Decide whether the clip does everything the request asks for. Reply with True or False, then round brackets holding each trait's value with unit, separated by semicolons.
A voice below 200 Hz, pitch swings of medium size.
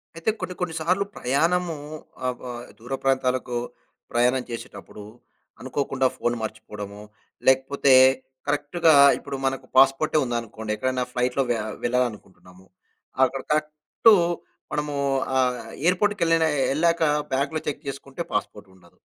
True (135 Hz; 4.2 semitones)